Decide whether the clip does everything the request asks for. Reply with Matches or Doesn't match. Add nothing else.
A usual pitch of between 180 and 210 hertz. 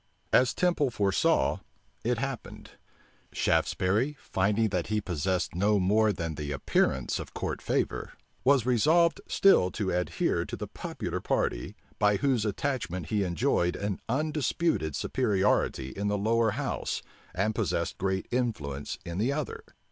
Doesn't match